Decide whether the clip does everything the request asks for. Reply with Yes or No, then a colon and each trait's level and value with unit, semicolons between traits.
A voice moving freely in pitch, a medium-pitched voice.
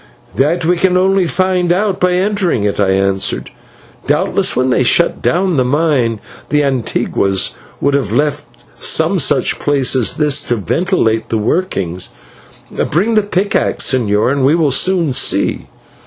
Yes: wide, 7.4 semitones; medium, 145 Hz